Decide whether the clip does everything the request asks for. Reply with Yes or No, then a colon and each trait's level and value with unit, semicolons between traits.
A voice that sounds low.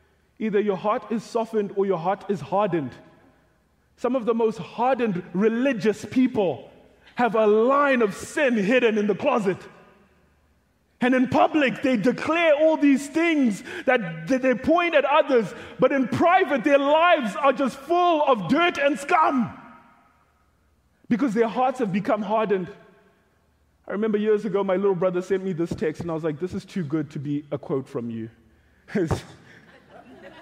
No: high, 220 Hz